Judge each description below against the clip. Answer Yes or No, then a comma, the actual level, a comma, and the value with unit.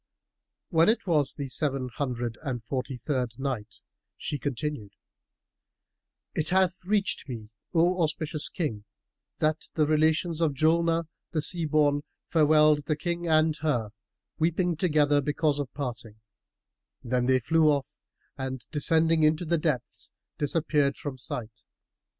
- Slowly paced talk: Yes, slow, 130 wpm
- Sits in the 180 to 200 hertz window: No, medium, 150 Hz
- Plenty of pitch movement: No, average, 3.6 semitones